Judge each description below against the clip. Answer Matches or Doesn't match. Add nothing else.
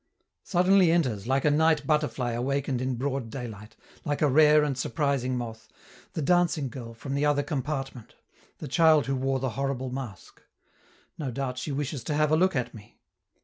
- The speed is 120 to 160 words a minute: Doesn't match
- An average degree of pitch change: Matches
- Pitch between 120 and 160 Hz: Matches